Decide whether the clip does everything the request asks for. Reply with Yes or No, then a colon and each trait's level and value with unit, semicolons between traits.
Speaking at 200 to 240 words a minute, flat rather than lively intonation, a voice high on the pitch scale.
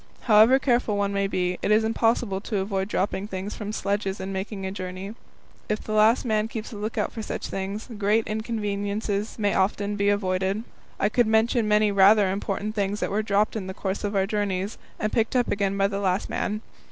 Yes: fast, 205 wpm; narrow, 1.7 semitones; high, 205 Hz